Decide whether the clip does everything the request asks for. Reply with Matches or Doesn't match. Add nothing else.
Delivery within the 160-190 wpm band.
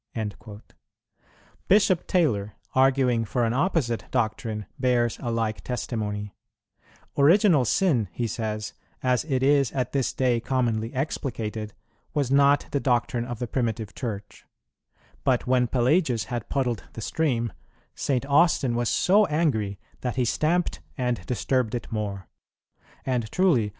Doesn't match